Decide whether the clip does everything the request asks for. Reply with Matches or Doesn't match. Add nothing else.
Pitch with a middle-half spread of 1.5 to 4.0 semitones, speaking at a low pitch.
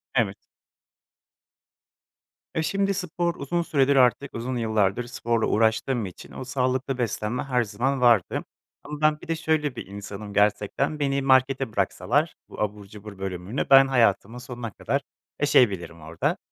Doesn't match